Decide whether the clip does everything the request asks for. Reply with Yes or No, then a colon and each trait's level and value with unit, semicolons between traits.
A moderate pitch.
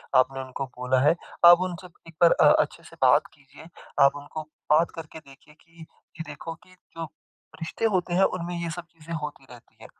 Yes: medium, 160 Hz